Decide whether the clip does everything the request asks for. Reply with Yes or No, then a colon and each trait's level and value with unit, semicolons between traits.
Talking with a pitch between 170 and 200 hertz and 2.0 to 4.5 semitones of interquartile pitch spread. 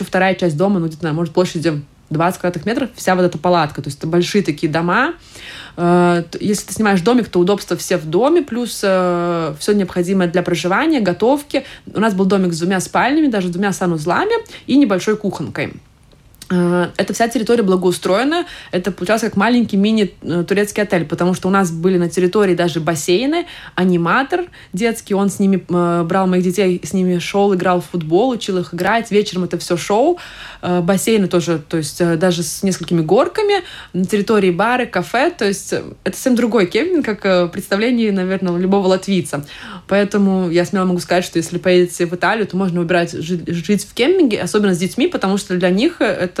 Yes: medium, 185 Hz; average, 2.9 semitones